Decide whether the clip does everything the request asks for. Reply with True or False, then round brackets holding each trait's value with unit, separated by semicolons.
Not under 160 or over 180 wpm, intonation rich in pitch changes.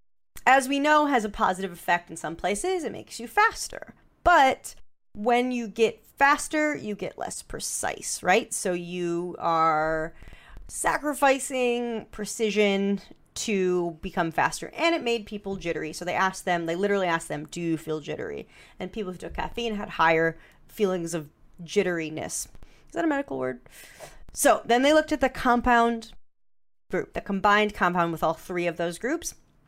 True (165 wpm; 5.9 semitones)